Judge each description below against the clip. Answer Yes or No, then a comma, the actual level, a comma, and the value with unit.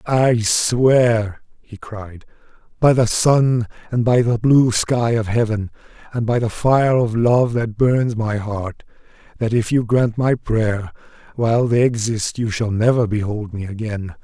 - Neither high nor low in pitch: No, low, 115 Hz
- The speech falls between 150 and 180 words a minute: Yes, average, 165 wpm